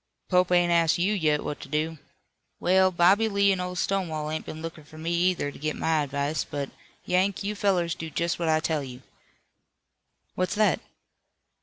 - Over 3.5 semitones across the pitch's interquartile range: No, average, 3.0 semitones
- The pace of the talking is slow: No, average, 185 wpm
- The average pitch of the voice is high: No, medium, 170 Hz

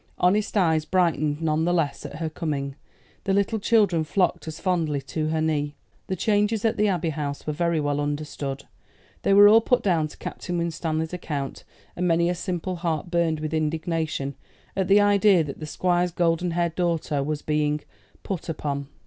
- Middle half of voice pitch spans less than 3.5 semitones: Yes, average, 3.0 semitones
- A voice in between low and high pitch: Yes, medium, 165 Hz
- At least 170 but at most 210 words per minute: Yes, average, 185 wpm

